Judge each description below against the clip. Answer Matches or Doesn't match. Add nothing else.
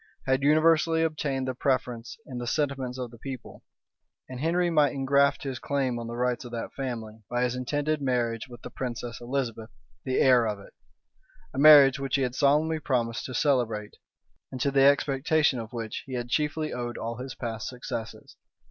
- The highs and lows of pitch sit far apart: Doesn't match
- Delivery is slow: Doesn't match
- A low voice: Matches